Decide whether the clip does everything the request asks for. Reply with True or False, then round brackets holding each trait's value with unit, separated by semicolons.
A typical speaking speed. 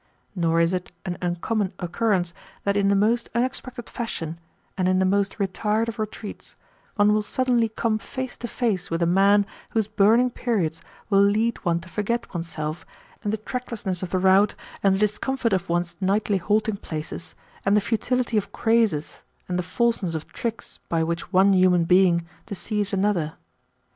True (175 wpm)